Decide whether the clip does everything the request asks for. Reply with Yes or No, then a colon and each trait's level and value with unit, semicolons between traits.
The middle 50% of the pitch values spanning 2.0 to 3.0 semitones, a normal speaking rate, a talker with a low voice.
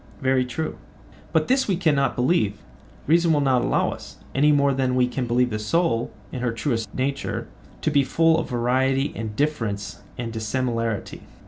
No: average, 4.2 semitones; average, 160 wpm; low, 130 Hz